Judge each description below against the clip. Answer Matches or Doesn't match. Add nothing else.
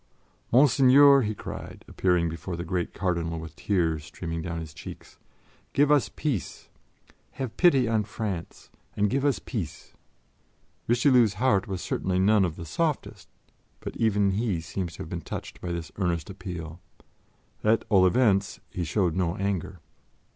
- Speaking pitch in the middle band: Doesn't match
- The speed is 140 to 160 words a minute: Matches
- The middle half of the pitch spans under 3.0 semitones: Doesn't match